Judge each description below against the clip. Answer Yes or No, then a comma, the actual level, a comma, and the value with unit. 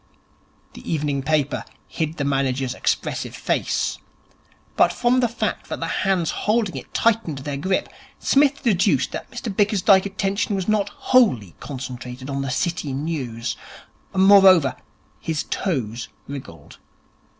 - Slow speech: Yes, slow, 130 wpm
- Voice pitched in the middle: Yes, medium, 160 Hz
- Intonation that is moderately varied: No, wide, 6.7 semitones